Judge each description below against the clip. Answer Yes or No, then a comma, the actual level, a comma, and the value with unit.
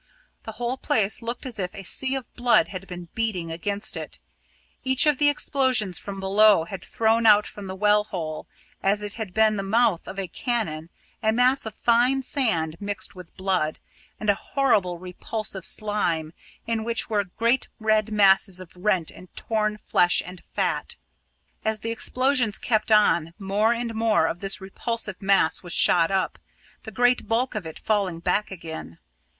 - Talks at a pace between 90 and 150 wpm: No, average, 180 wpm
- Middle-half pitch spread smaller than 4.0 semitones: Yes, average, 3.6 semitones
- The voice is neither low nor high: No, high, 210 Hz